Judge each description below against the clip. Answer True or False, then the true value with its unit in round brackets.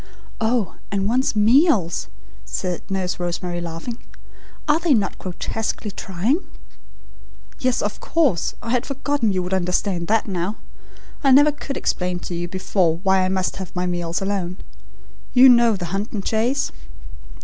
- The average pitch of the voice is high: True (195 Hz)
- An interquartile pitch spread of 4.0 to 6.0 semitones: True (4.9 semitones)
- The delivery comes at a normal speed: True (160 wpm)